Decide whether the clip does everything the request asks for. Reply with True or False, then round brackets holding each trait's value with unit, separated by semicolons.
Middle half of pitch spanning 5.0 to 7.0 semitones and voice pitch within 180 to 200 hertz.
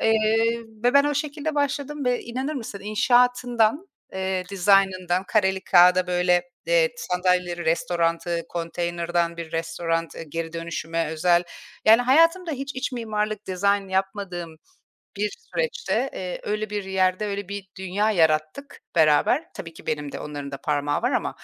True (5.6 semitones; 190 Hz)